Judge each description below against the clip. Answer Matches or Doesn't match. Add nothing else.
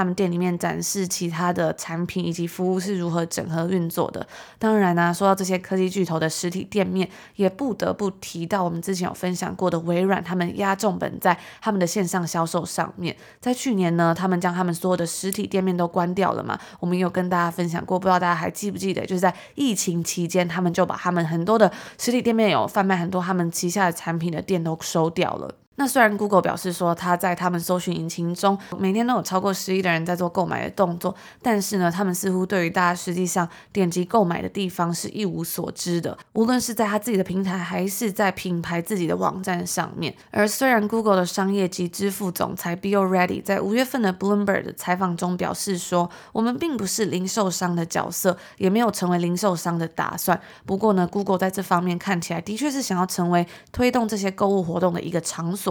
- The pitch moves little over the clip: Matches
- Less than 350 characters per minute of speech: Doesn't match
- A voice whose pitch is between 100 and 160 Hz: Doesn't match